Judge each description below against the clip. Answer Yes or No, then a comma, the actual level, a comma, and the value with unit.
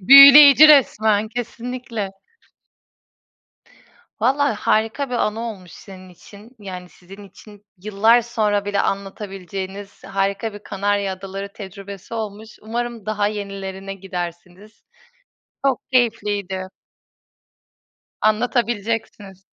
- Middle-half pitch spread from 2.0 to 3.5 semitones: Yes, average, 2.7 semitones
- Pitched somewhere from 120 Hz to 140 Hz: No, high, 205 Hz